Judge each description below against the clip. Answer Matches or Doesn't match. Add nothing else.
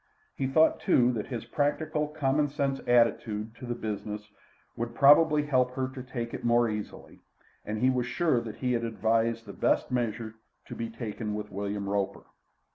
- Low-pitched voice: Matches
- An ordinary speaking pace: Matches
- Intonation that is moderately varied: Matches